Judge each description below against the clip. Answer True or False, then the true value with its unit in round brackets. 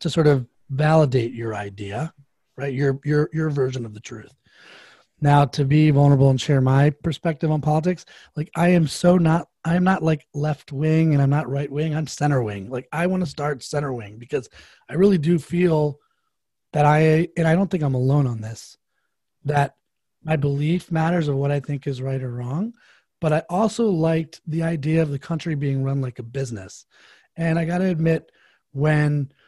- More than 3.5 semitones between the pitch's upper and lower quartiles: False (3.0 semitones)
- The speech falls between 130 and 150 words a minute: False (195 wpm)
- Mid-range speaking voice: True (150 Hz)